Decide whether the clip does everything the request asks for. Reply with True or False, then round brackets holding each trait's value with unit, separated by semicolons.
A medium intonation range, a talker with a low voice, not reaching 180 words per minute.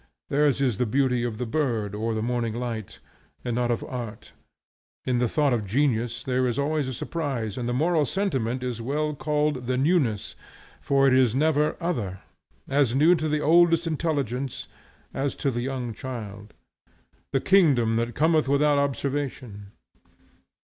True (3.9 semitones; 130 Hz; 165 wpm)